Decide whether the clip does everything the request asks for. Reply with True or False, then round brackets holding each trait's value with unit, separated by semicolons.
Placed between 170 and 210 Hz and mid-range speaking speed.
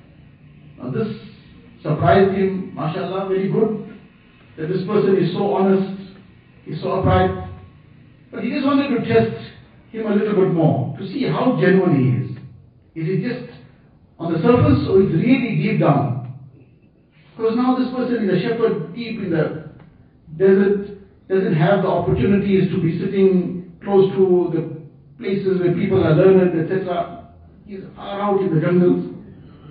True (185 Hz; 155 wpm)